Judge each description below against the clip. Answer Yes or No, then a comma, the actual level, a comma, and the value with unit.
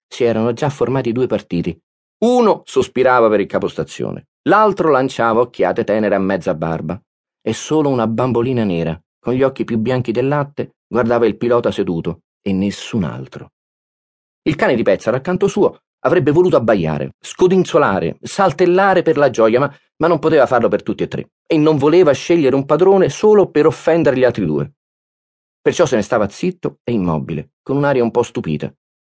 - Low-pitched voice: Yes, low, 125 Hz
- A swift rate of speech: Yes, fast, 175 wpm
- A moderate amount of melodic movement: No, wide, 6.6 semitones